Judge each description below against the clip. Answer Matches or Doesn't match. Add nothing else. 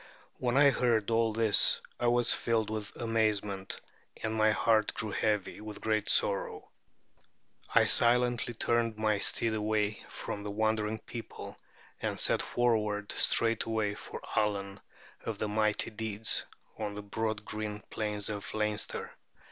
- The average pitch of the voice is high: Doesn't match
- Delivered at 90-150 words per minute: Matches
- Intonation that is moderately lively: Doesn't match